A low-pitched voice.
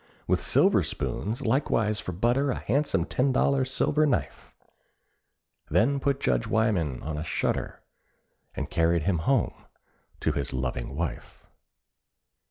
Yes: low, 105 Hz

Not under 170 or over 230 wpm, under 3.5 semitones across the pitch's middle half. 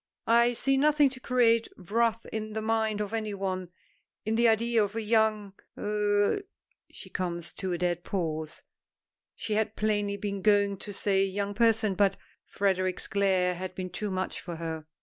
Yes: average, 175 wpm; average, 2.9 semitones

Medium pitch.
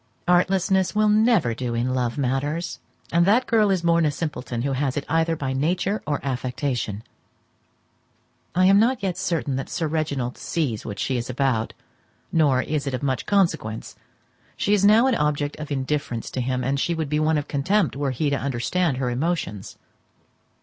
Yes: medium, 145 Hz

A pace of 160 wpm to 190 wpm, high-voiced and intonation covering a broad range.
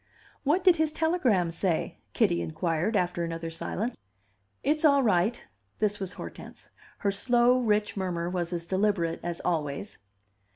No: average, 140 wpm; high, 195 Hz; wide, 6.0 semitones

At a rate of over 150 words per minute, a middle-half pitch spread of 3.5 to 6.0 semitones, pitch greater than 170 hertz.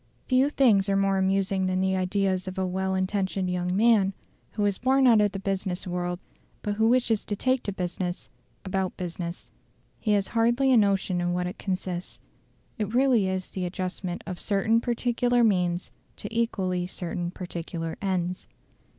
No: average, 170 wpm; average, 2.9 semitones; high, 190 Hz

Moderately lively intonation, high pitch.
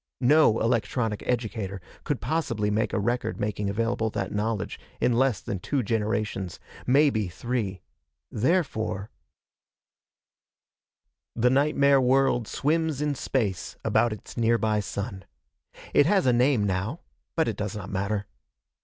No: average, 4.2 semitones; low, 115 Hz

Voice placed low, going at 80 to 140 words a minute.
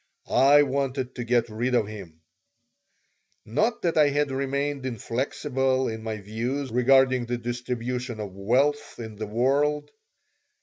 Yes: low, 125 Hz; slow, 135 wpm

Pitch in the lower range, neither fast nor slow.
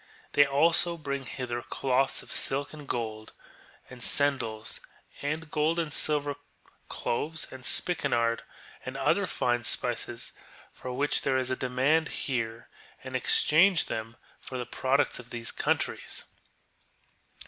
No: low, 130 Hz; slow, 130 wpm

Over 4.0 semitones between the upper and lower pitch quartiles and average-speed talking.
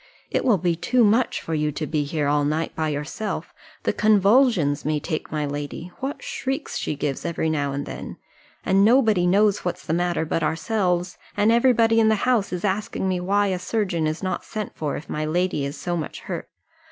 No: wide, 5.6 semitones; fast, 210 wpm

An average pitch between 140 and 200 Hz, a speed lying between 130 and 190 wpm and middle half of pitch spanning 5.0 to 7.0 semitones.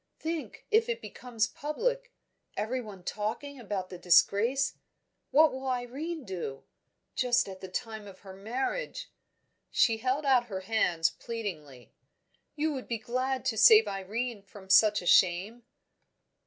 No: high, 230 Hz; average, 140 wpm; wide, 5.5 semitones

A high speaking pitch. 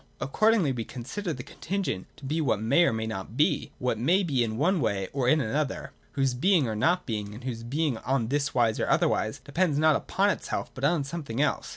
No: low, 135 Hz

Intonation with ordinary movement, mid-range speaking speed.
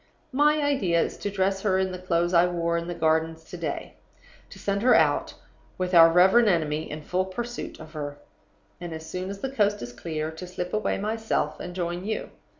No: average, 3.4 semitones; fast, 210 wpm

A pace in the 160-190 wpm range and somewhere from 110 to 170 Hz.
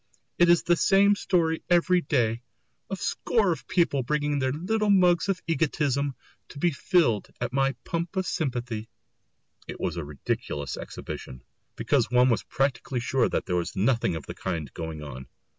Yes: average, 170 wpm; medium, 140 Hz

